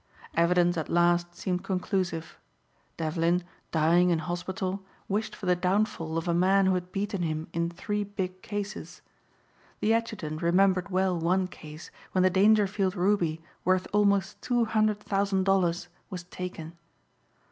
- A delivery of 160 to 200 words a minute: No, average, 145 wpm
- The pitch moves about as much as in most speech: No, narrow, 2.3 semitones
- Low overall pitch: No, medium, 185 Hz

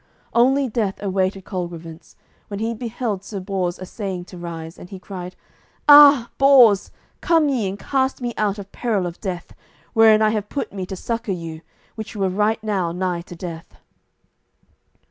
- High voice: Yes, high, 200 Hz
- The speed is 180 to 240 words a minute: No, average, 165 wpm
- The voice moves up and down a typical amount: Yes, average, 4.0 semitones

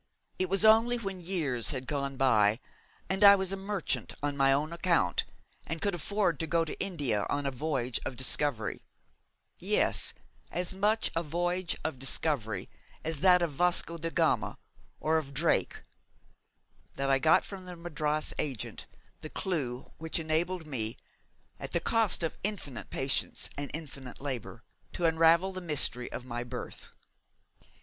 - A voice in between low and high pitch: Yes, medium, 160 Hz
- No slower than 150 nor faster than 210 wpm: Yes, average, 155 wpm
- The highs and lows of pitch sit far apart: No, average, 4.9 semitones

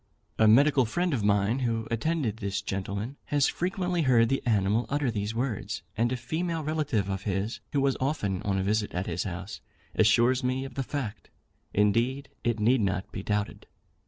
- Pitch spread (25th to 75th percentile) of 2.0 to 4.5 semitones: No, average, 4.9 semitones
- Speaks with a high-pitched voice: No, low, 115 Hz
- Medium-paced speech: Yes, average, 185 wpm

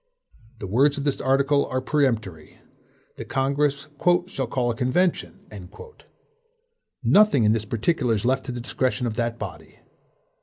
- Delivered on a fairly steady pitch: No, average, 3.2 semitones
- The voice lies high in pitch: No, low, 130 Hz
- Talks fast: No, average, 145 wpm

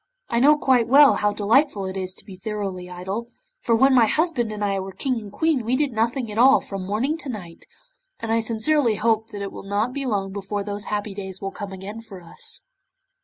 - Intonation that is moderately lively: Yes, average, 4.3 semitones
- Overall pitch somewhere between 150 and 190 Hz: No, high, 215 Hz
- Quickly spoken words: Yes, fast, 225 wpm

